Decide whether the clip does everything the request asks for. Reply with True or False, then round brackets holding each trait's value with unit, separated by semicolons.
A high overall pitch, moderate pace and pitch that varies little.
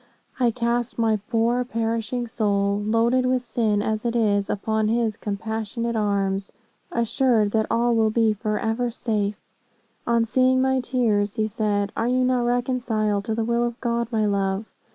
True (225 Hz; 160 wpm; 2.1 semitones)